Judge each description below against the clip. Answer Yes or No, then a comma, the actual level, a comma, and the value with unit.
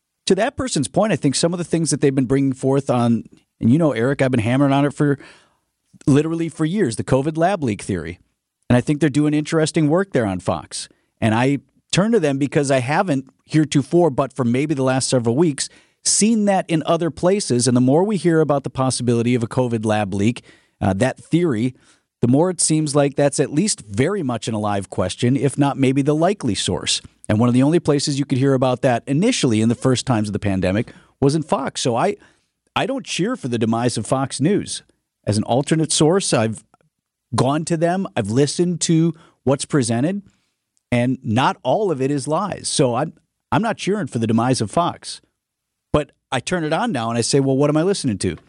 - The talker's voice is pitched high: No, medium, 140 Hz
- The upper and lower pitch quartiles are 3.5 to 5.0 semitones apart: Yes, average, 4.6 semitones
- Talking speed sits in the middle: No, fast, 220 wpm